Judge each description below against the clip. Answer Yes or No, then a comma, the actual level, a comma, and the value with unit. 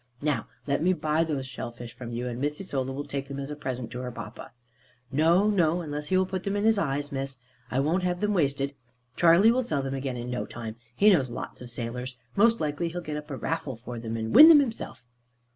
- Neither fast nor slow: No, fast, 240 wpm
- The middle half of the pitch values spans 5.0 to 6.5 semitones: Yes, wide, 5.6 semitones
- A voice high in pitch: No, medium, 145 Hz